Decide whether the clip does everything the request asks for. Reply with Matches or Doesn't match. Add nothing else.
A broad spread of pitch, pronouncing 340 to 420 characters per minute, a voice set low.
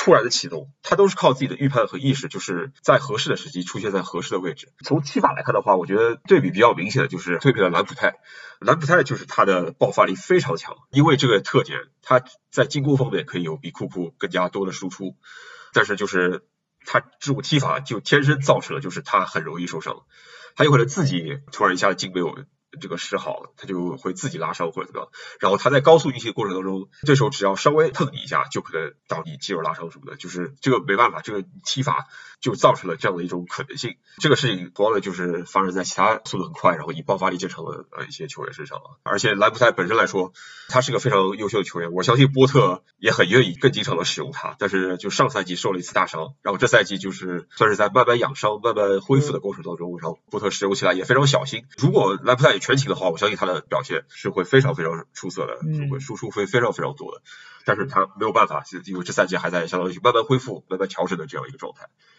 Matches